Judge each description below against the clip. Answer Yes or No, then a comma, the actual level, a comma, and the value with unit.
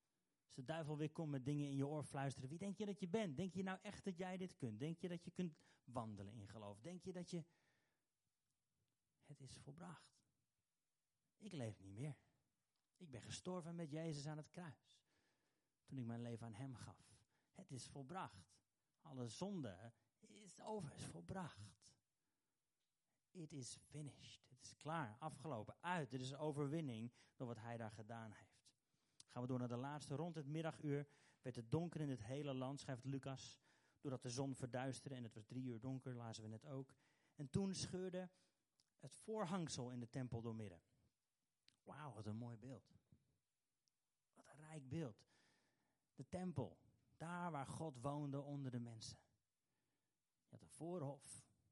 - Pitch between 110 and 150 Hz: Yes, medium, 140 Hz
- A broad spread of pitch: No, average, 4.6 semitones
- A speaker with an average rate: Yes, average, 175 wpm